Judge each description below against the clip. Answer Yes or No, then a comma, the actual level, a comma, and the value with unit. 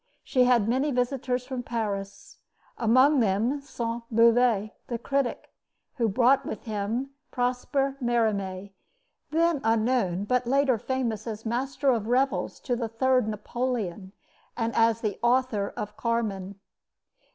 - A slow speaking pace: Yes, slow, 130 wpm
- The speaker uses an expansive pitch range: No, average, 3.0 semitones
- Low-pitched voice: No, high, 235 Hz